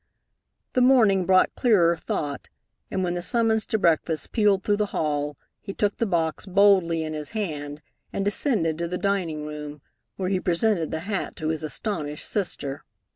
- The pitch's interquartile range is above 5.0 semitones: No, average, 4.7 semitones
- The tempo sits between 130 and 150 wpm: No, average, 175 wpm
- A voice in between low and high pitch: Yes, medium, 180 Hz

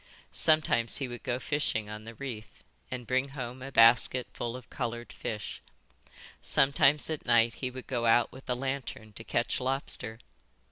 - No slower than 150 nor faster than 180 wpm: Yes, average, 170 wpm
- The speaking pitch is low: Yes, low, 125 Hz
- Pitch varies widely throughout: No, narrow, 2.6 semitones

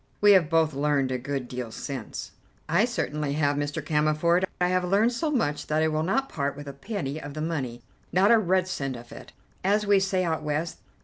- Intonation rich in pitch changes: No, average, 4.7 semitones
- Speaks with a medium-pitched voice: Yes, medium, 155 Hz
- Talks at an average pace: No, fast, 215 wpm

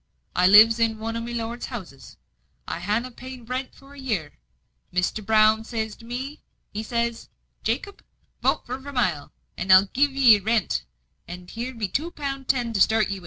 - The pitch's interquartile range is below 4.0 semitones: Yes, average, 3.5 semitones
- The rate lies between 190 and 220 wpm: Yes, average, 195 wpm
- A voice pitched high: Yes, high, 230 Hz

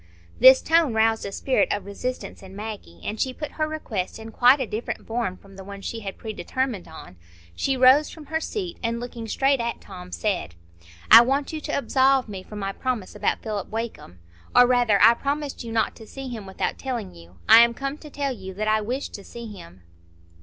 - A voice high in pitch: Yes, high, 230 Hz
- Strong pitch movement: No, average, 4.7 semitones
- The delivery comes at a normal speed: No, fast, 215 wpm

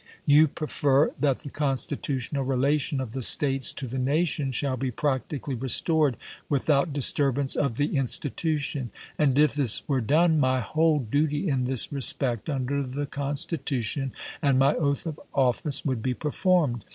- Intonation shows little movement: Yes, narrow, 2.2 semitones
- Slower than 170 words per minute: Yes, average, 155 wpm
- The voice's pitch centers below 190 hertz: Yes, medium, 140 Hz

